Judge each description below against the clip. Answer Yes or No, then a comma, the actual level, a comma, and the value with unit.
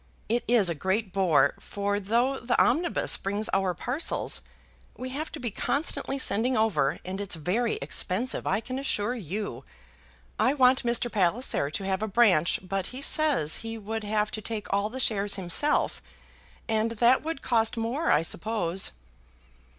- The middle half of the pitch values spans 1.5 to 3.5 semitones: No, average, 4.2 semitones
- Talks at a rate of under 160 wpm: No, average, 165 wpm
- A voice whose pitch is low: No, high, 220 Hz